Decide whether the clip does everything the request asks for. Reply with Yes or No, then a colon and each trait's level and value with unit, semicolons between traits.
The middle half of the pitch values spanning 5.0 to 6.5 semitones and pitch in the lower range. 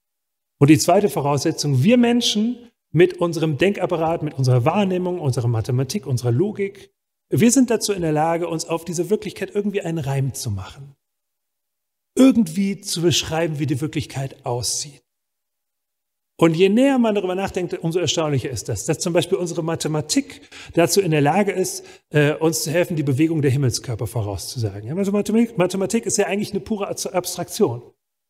No: average, 5.3 semitones; medium, 170 Hz